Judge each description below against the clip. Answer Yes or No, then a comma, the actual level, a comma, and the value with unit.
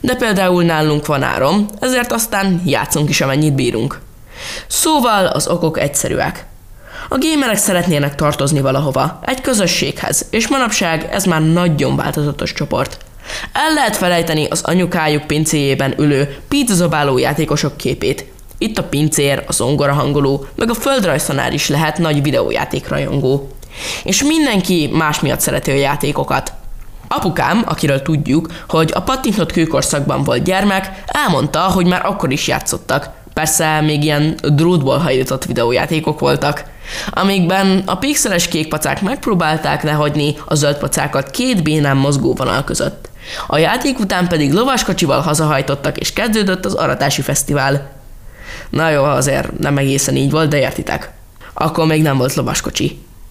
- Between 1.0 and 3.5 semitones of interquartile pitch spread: No, average, 4.6 semitones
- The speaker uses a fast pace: No, average, 135 wpm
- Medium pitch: Yes, medium, 155 Hz